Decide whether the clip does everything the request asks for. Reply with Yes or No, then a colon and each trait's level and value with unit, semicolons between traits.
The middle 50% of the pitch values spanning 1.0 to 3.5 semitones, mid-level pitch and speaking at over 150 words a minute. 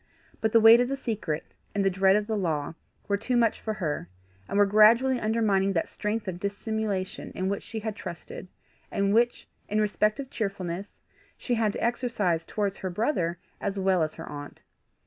No: average, 2.9 semitones; high, 205 Hz; average, 190 wpm